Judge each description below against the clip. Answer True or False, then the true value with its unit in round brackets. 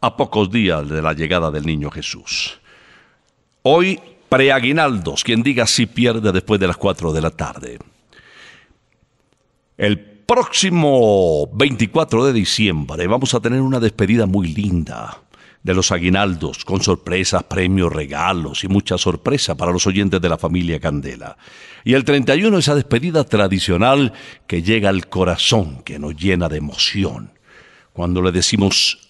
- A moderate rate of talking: True (140 wpm)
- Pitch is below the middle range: True (95 Hz)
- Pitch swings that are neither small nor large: False (5.7 semitones)